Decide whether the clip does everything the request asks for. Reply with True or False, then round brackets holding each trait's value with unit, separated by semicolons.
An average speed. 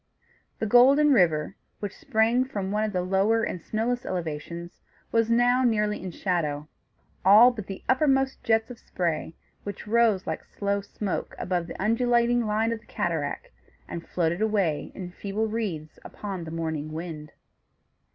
True (155 wpm)